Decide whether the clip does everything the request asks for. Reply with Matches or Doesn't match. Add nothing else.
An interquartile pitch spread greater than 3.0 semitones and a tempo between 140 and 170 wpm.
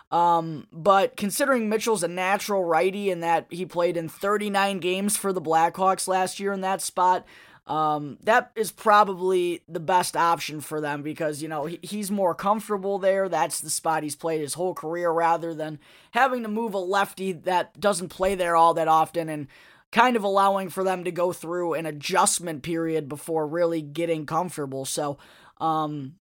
Doesn't match